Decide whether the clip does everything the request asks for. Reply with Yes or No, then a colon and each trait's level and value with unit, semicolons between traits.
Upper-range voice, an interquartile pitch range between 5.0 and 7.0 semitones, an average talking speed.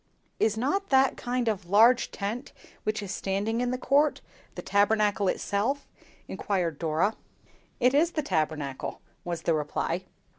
Yes: high, 210 Hz; wide, 5.5 semitones; average, 145 wpm